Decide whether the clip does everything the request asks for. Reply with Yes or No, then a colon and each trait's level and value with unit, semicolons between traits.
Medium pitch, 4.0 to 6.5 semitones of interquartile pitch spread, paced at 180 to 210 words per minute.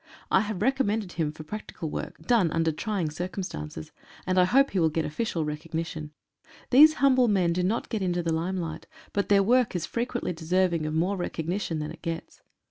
Yes: medium, 180 Hz; average, 4.6 semitones; average, 190 wpm